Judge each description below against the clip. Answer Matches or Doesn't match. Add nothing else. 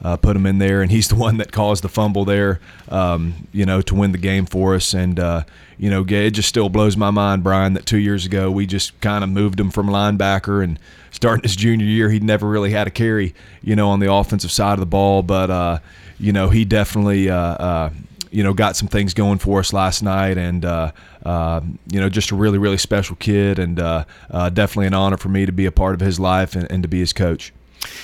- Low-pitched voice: Matches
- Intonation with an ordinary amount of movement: Doesn't match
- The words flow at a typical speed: Doesn't match